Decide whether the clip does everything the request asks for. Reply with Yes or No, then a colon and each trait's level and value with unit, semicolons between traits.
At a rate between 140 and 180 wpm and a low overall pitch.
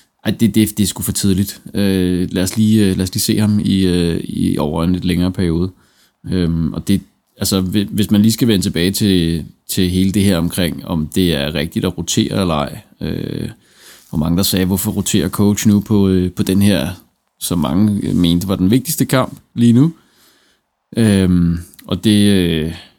No: average, 195 wpm; very low, 95 Hz